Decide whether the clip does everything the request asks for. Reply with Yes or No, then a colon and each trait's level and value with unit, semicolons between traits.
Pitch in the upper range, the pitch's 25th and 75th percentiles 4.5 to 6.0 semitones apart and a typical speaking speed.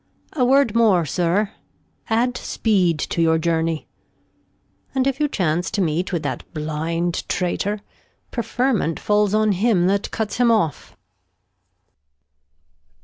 No: high, 195 Hz; average, 5.3 semitones; slow, 125 wpm